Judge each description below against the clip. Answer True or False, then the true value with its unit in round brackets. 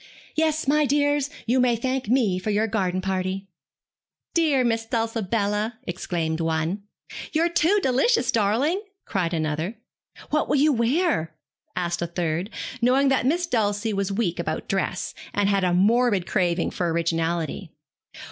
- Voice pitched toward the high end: True (210 Hz)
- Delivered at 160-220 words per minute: False (145 wpm)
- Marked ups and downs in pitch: True (6.6 semitones)